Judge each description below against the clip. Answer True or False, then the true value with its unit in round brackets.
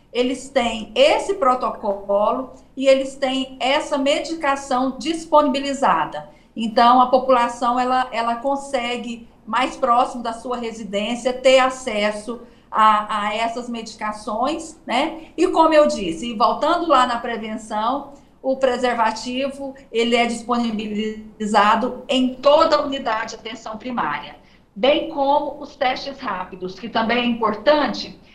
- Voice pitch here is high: True (245 Hz)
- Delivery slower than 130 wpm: True (120 wpm)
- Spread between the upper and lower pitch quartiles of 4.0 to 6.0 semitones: False (3.4 semitones)